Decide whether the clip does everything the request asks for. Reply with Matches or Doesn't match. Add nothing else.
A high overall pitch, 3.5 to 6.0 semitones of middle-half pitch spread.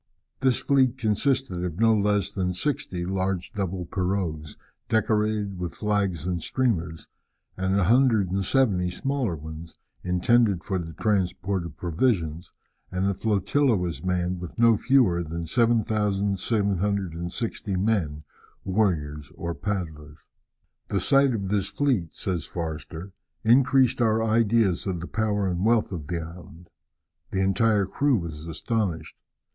Doesn't match